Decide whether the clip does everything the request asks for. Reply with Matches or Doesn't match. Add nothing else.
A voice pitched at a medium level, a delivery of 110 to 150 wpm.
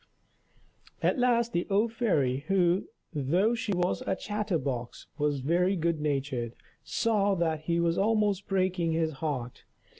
Matches